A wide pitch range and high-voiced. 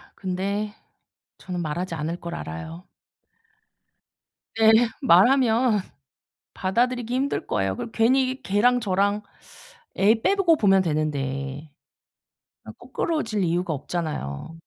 Yes: wide, 6.8 semitones; high, 195 Hz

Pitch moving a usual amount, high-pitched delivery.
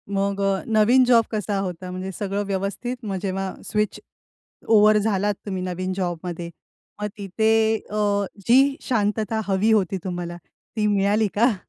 No: narrow, 2.3 semitones; high, 205 Hz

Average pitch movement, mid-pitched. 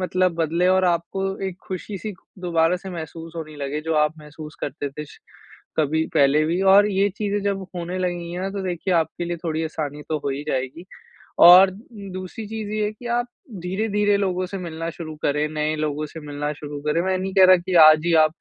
Yes: average, 3.5 semitones; medium, 170 Hz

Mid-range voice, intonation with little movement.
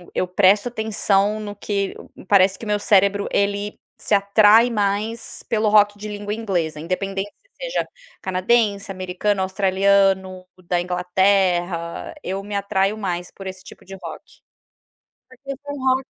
No: high, 200 Hz; narrow, 1.9 semitones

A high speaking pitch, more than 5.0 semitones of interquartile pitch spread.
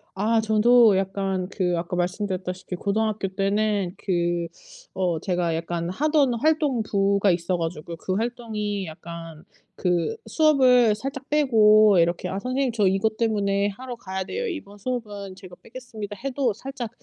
No: high, 205 Hz; average, 4.5 semitones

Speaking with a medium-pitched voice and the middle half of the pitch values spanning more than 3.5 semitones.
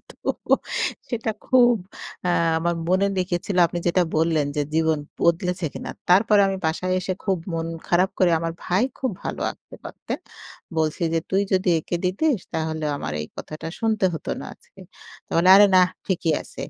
No: medium, 180 Hz; average, 2.9 semitones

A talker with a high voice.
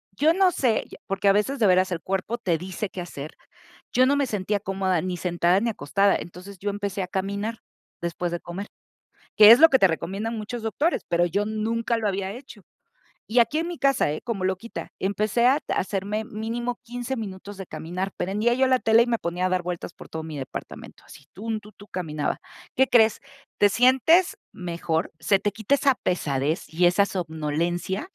Yes: high, 200 Hz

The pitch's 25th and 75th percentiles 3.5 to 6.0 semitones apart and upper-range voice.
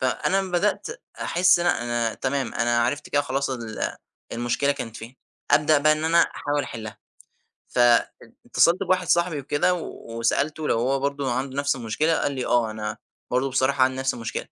No: average, 4.3 semitones; low, 135 Hz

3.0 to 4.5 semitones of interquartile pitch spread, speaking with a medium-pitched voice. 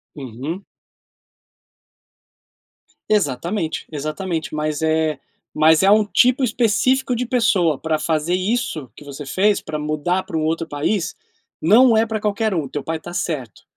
No: wide, 5.5 semitones; medium, 165 Hz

